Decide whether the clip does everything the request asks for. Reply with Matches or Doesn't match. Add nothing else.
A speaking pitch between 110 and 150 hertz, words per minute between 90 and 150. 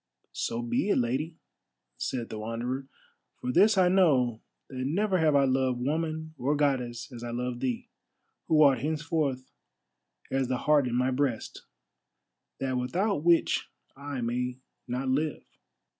Matches